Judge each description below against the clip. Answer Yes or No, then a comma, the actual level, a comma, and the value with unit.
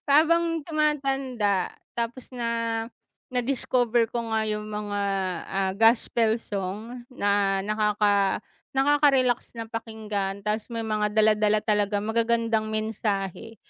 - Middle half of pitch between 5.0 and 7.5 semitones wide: No, narrow, 2.5 semitones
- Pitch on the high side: Yes, high, 225 Hz